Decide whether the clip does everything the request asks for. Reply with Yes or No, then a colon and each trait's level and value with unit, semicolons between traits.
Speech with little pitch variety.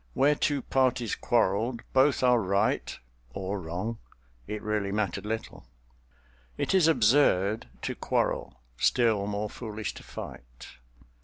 No: average, 4.6 semitones